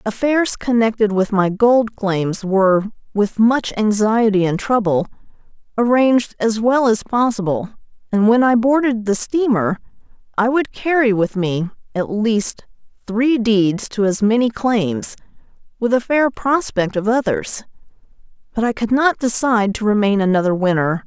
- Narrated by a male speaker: No, female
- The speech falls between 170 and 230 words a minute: No, average, 145 wpm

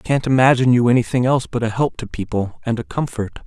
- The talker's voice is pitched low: Yes, low, 120 Hz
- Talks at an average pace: No, fast, 240 wpm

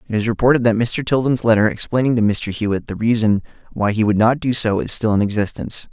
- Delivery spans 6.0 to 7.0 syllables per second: Yes, 6.2 syllables/s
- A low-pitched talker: Yes, low, 110 Hz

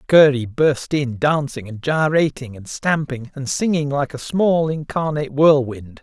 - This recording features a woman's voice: No, male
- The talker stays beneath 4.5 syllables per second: Yes, 4.3 syllables/s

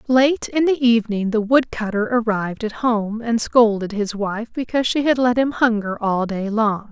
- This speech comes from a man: No, female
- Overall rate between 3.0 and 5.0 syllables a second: Yes, 4.8 syllables/s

